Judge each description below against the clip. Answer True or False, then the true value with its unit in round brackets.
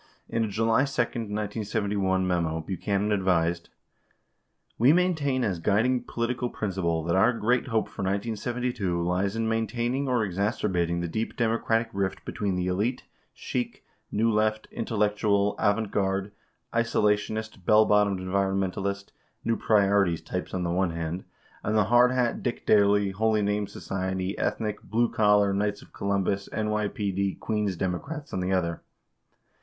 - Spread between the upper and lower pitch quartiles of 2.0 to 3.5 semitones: True (2.9 semitones)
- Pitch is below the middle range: True (105 Hz)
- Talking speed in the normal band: True (145 wpm)